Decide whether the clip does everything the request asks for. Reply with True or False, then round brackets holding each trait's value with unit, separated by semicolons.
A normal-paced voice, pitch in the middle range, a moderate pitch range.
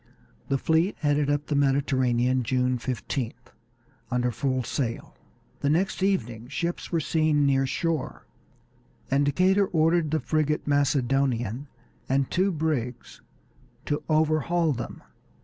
False (120 wpm; 145 Hz; 3.5 semitones)